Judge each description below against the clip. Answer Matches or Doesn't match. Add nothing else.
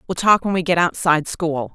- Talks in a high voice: Doesn't match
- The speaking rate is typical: Doesn't match